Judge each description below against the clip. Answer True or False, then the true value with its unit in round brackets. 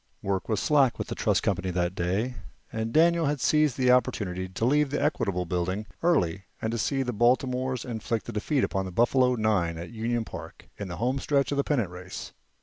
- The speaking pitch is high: False (115 Hz)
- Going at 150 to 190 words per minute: False (200 wpm)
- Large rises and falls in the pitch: True (6.0 semitones)